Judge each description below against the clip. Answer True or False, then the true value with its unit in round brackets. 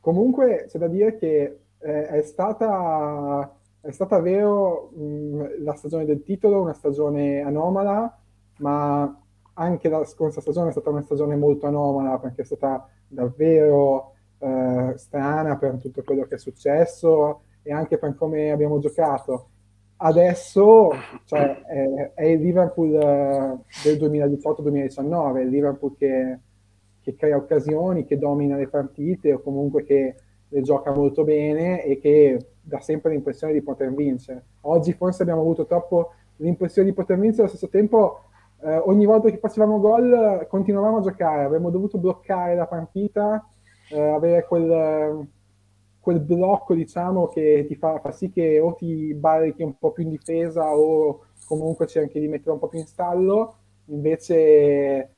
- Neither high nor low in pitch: True (150 Hz)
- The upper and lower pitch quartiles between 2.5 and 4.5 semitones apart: True (3.5 semitones)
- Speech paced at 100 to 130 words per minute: False (150 wpm)